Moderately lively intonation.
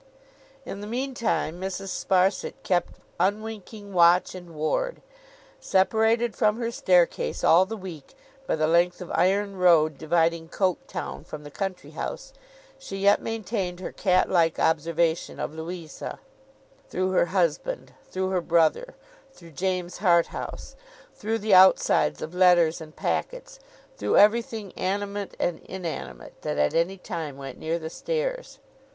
Yes: average, 3.5 semitones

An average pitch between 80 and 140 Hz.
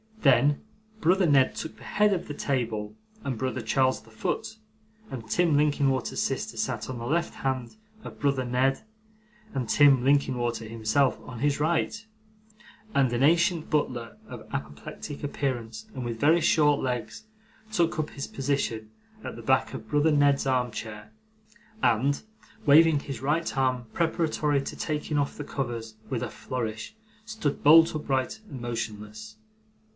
Yes: low, 135 Hz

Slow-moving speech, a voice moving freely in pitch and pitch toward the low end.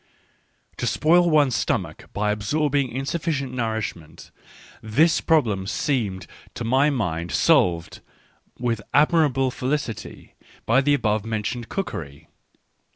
Yes: slow, 115 wpm; wide, 5.7 semitones; low, 125 Hz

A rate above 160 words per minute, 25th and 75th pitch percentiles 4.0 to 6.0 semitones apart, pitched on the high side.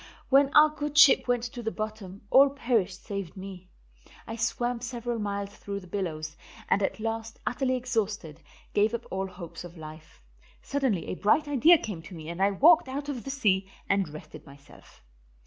Yes: average, 180 wpm; average, 5.2 semitones; high, 215 Hz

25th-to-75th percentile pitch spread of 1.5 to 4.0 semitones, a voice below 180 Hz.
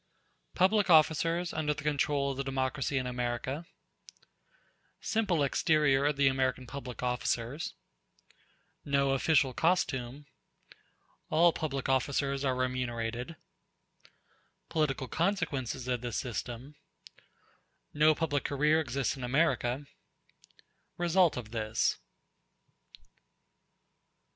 Yes: average, 3.5 semitones; medium, 140 Hz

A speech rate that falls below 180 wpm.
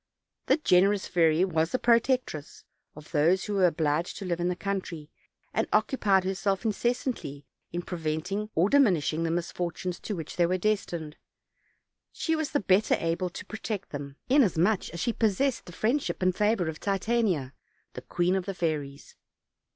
Yes: average, 165 wpm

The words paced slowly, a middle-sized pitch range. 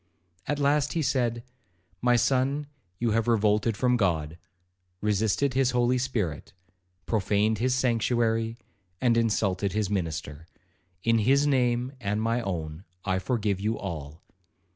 Yes: slow, 125 wpm; average, 4.2 semitones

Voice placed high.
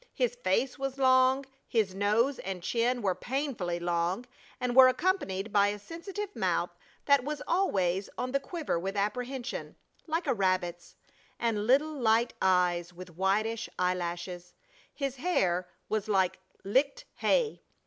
Yes: high, 225 Hz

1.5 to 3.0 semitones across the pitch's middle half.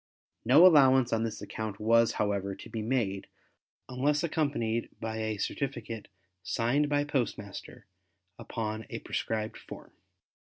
No: average, 4.0 semitones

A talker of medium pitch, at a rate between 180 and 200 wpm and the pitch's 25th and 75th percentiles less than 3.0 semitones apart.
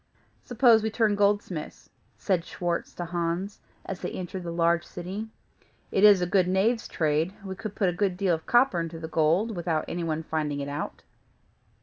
No: medium, 180 Hz; average, 190 wpm; average, 3.4 semitones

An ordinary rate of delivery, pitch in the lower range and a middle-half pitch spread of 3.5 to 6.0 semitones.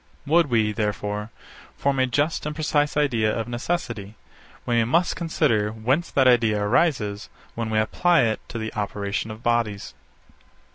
Yes: average, 150 wpm; low, 115 Hz; average, 5.2 semitones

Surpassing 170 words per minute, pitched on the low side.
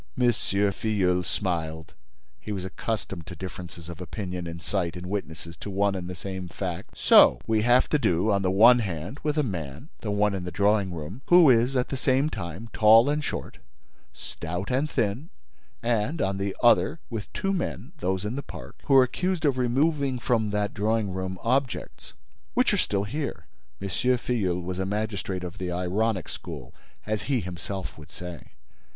Yes: average, 180 wpm; low, 100 Hz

